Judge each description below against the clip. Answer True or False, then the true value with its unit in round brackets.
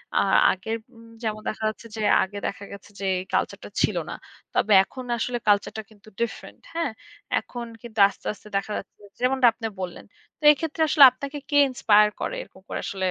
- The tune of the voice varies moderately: True (3.8 semitones)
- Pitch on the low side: False (220 Hz)